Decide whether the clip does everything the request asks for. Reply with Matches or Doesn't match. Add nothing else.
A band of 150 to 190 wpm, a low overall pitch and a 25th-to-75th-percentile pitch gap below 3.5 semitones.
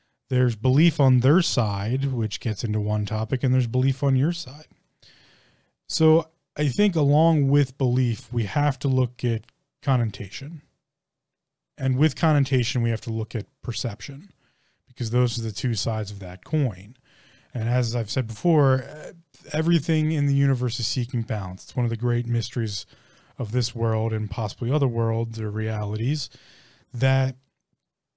Doesn't match